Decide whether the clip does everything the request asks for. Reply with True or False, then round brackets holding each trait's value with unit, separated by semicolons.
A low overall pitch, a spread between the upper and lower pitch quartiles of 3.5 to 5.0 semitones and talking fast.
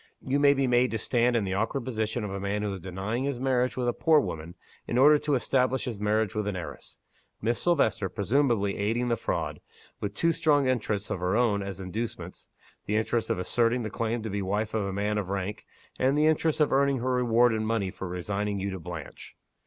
True (110 Hz; 4.1 semitones; 230 wpm)